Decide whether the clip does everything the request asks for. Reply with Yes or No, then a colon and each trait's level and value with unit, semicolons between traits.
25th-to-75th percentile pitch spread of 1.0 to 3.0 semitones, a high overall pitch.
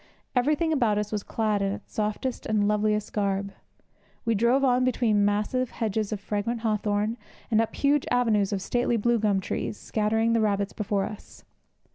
Yes: narrow, 2.5 semitones; high, 215 Hz